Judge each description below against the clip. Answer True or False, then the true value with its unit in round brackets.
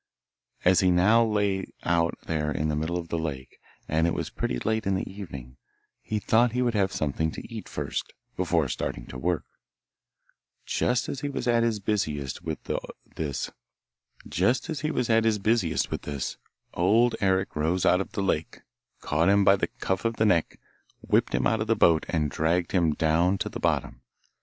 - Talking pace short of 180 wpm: True (170 wpm)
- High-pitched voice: False (90 Hz)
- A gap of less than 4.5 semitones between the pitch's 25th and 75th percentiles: False (5.3 semitones)